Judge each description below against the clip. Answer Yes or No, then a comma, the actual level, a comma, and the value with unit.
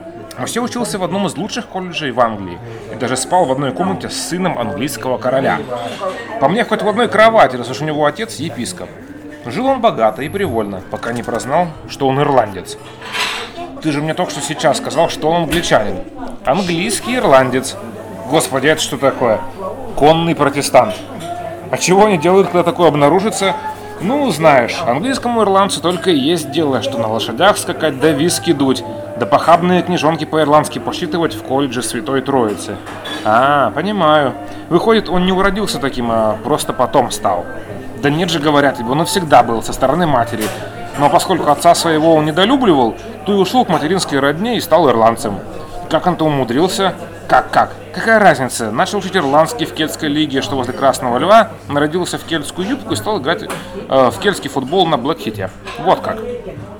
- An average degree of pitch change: No, wide, 5.9 semitones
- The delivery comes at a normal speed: No, fast, 170 wpm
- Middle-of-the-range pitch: Yes, medium, 155 Hz